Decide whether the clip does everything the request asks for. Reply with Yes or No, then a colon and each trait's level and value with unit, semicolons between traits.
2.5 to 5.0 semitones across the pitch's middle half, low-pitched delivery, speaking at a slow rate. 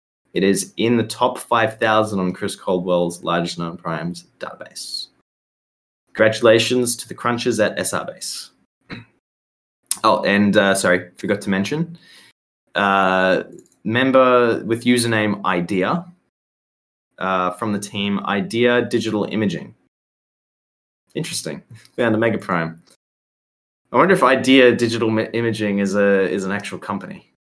Yes: average, 4.5 semitones; low, 105 Hz; slow, 120 wpm